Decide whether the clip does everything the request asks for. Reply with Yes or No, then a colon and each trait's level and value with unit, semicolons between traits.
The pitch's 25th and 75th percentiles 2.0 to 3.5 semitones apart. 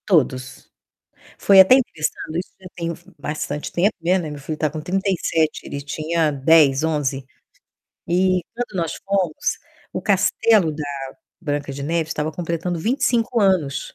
No: average, 4.0 semitones